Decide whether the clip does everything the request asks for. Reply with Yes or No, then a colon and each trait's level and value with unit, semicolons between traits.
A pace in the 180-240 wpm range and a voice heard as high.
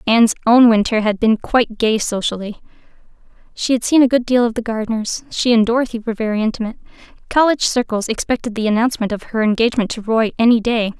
Yes: average, 190 wpm; high, 225 Hz